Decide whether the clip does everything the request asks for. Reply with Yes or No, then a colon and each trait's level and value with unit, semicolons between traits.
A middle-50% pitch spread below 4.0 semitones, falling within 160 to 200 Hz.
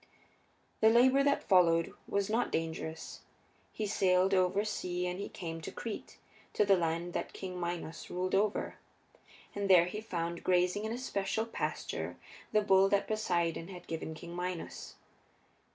Yes: average, 3.2 semitones; medium, 185 Hz